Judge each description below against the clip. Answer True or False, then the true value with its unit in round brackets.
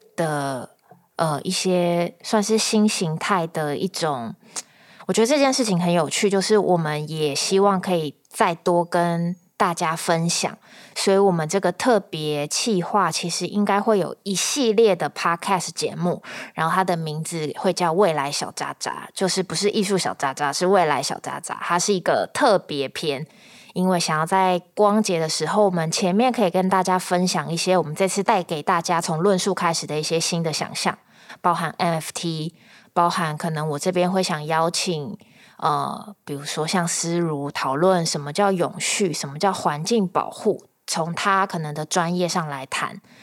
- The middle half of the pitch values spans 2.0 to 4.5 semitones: True (3.3 semitones)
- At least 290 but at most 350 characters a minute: False (265 characters per minute)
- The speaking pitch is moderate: True (175 Hz)